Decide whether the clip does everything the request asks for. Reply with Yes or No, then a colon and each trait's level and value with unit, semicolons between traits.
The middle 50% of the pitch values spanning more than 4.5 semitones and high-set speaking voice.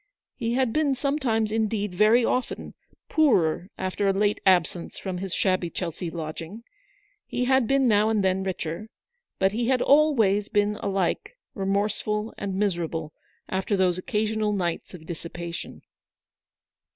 No: average, 3.5 semitones; high, 205 Hz